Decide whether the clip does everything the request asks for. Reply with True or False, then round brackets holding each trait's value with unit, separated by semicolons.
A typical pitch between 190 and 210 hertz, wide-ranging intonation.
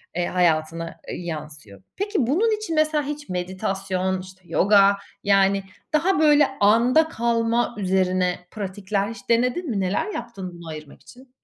True (200 Hz; 5.9 semitones)